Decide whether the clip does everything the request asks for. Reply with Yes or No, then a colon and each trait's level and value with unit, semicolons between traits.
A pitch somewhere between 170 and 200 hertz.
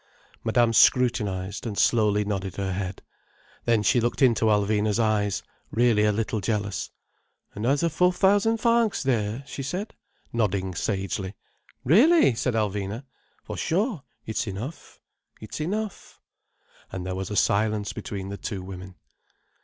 No: low, 110 Hz